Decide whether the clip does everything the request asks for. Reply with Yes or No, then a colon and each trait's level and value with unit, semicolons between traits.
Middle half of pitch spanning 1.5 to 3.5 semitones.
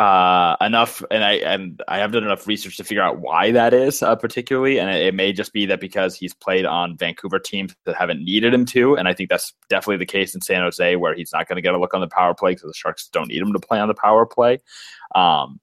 No: average, 4.3 semitones